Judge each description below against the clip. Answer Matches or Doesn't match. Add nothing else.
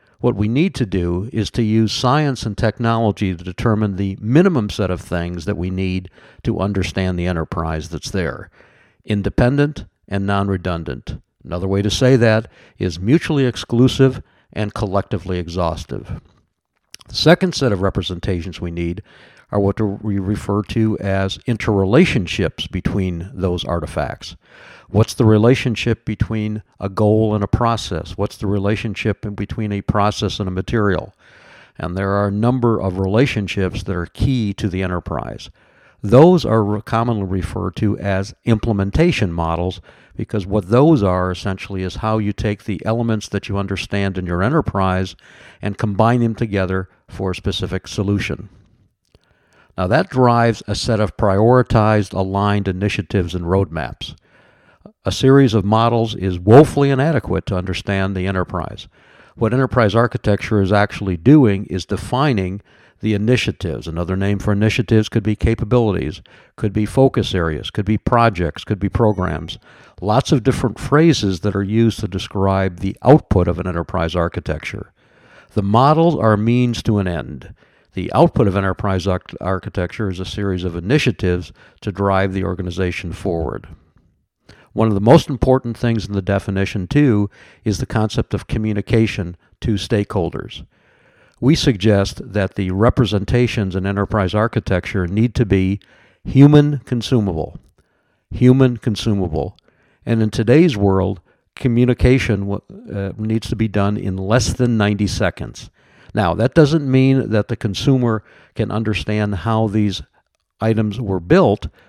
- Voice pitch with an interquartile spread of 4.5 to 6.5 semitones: Doesn't match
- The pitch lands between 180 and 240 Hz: Doesn't match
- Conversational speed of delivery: Matches